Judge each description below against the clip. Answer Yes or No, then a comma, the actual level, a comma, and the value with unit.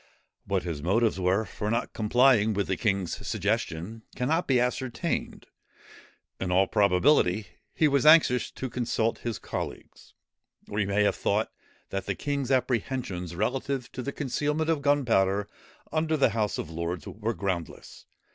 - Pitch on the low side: Yes, low, 110 Hz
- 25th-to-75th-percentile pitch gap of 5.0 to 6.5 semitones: Yes, wide, 5.4 semitones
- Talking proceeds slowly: No, average, 150 wpm